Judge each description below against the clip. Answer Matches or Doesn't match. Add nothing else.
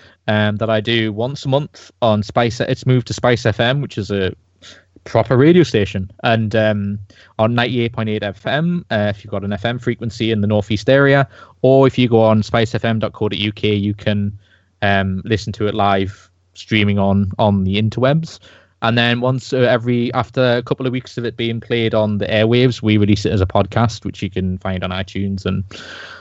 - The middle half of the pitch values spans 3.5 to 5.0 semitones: Doesn't match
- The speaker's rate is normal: Matches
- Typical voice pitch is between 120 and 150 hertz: Doesn't match